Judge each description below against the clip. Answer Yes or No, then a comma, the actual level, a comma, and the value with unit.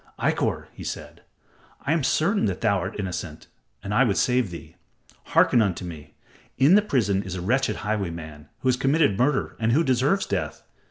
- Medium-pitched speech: No, low, 110 Hz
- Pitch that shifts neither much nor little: No, wide, 6.5 semitones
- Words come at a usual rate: Yes, average, 180 wpm